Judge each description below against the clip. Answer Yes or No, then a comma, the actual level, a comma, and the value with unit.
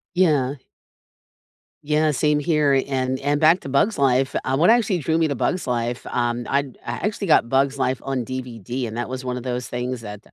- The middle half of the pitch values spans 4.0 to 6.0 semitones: No, average, 3.3 semitones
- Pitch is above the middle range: No, low, 135 Hz